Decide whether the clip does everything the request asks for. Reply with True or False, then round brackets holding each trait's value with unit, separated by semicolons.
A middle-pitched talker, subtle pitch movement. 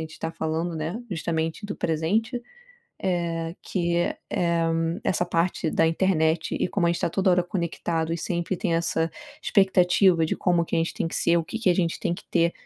True (170 Hz; 1.7 semitones)